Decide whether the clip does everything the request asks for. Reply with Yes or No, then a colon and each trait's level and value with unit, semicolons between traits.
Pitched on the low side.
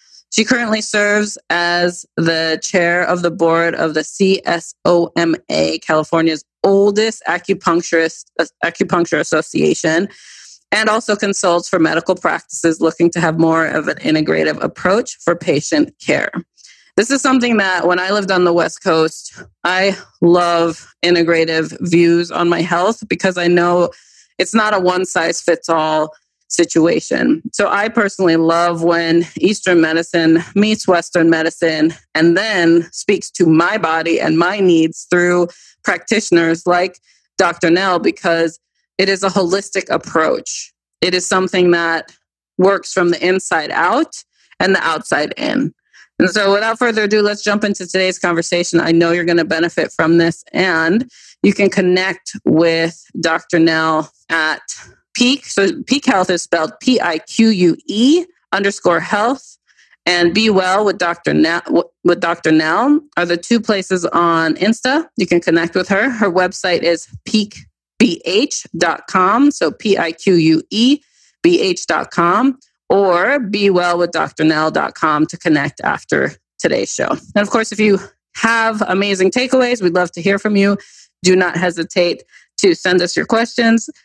No: medium, 180 Hz